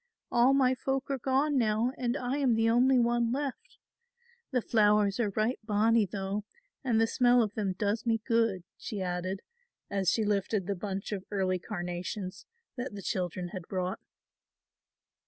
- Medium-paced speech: Yes, average, 165 wpm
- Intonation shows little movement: No, average, 4.0 semitones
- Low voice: No, high, 215 Hz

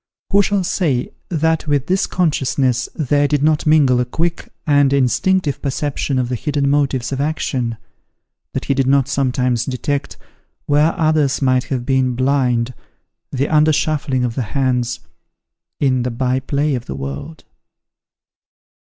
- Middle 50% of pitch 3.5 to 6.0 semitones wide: No, average, 2.9 semitones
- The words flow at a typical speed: Yes, average, 150 wpm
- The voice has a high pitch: No, medium, 140 Hz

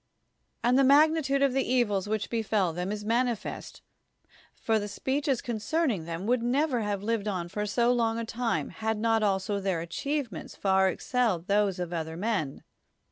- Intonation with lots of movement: No, average, 4.2 semitones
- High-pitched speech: Yes, high, 220 Hz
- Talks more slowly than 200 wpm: Yes, average, 180 wpm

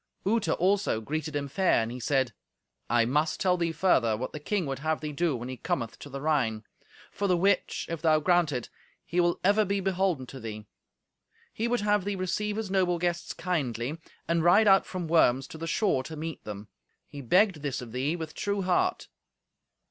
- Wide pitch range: Yes, wide, 5.7 semitones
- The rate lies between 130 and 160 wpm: No, fast, 205 wpm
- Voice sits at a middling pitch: Yes, medium, 160 Hz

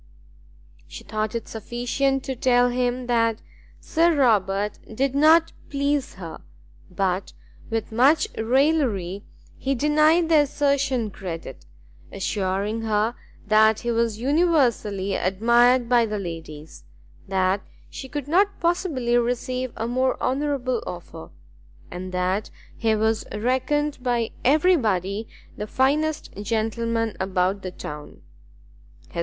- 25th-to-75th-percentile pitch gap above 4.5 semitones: Yes, average, 5.1 semitones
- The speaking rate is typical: No, slow, 115 wpm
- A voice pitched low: No, high, 235 Hz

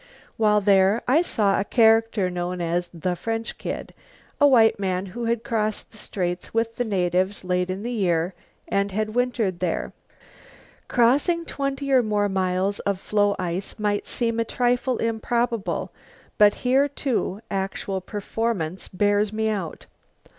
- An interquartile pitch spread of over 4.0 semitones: No, average, 3.7 semitones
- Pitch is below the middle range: No, high, 210 Hz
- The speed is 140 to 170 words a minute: Yes, average, 150 wpm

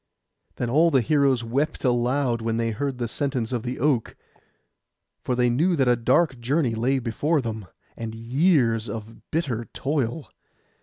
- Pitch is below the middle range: Yes, low, 125 Hz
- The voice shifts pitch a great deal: No, average, 3.6 semitones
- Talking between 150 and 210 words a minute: Yes, average, 160 wpm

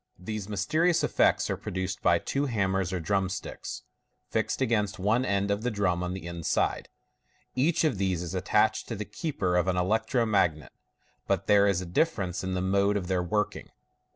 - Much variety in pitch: No, average, 3.0 semitones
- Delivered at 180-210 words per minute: Yes, average, 185 wpm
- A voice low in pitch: Yes, low, 100 Hz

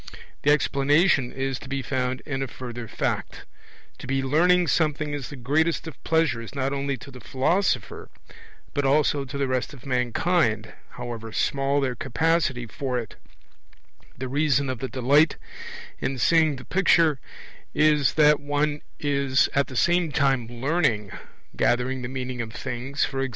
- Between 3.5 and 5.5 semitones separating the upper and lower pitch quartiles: No, average, 2.9 semitones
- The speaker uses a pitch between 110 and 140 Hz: Yes, low, 135 Hz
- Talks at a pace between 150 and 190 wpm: Yes, average, 155 wpm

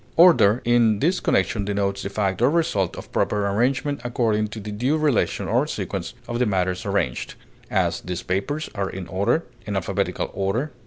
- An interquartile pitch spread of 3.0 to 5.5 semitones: Yes, average, 4.2 semitones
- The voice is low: Yes, low, 105 Hz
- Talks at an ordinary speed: Yes, average, 175 wpm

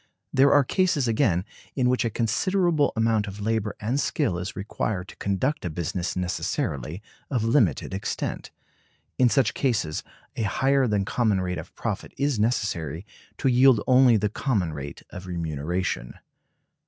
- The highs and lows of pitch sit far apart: Yes, wide, 6.0 semitones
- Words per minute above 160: No, average, 155 wpm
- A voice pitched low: Yes, low, 110 Hz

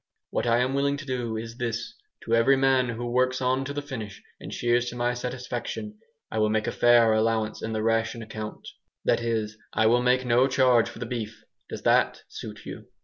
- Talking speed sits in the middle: No, fast, 210 wpm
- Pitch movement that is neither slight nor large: No, narrow, 2.2 semitones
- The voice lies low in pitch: Yes, low, 120 Hz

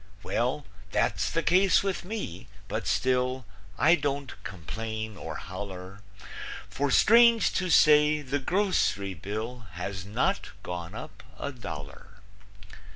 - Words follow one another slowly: Yes, slow, 120 wpm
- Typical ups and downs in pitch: No, wide, 7.6 semitones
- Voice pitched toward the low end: Yes, low, 125 Hz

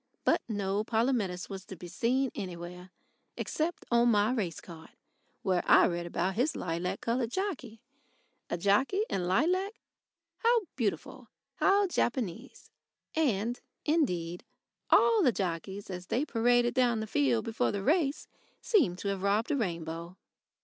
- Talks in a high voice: Yes, high, 215 Hz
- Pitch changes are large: Yes, wide, 6.4 semitones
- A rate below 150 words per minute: Yes, average, 140 wpm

